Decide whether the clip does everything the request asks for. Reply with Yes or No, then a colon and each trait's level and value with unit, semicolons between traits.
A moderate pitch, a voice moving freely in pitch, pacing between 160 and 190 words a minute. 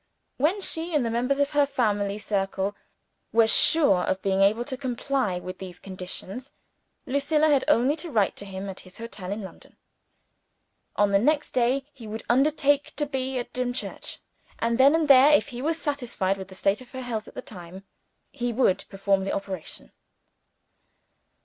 No: high, 240 Hz; wide, 6.0 semitones; average, 180 wpm